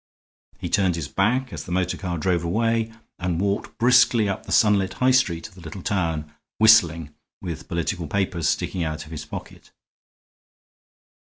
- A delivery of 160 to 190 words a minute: Yes, average, 165 wpm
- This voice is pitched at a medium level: No, very low, 95 Hz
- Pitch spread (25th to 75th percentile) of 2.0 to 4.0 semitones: No, average, 4.4 semitones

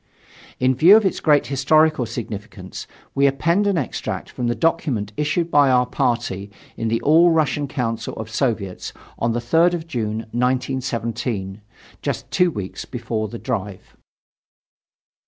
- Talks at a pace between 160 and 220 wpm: No, average, 145 wpm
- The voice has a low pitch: Yes, low, 125 Hz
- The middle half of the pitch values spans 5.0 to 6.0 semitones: Yes, wide, 5.4 semitones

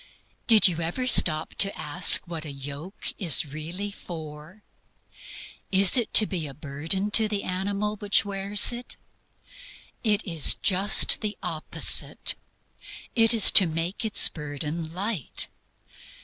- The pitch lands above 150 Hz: Yes, medium, 185 Hz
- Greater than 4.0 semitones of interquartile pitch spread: Yes, average, 4.8 semitones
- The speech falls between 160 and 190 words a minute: No, slow, 135 wpm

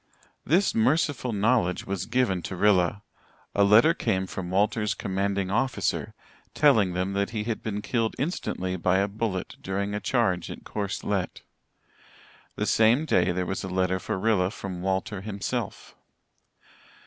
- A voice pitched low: Yes, low, 100 Hz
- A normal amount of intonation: Yes, average, 3.1 semitones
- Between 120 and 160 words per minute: Yes, average, 150 wpm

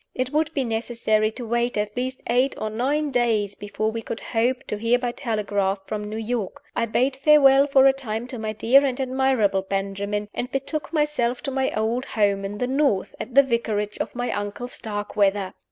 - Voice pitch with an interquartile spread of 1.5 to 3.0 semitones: No, average, 4.0 semitones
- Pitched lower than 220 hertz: No, high, 235 Hz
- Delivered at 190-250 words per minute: Yes, average, 200 wpm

